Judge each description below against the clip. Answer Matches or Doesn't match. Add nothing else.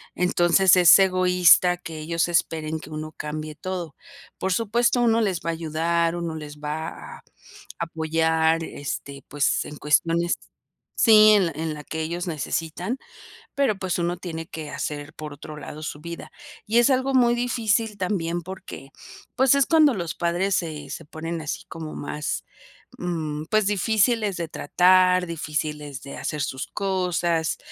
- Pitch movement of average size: Matches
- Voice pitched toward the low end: Doesn't match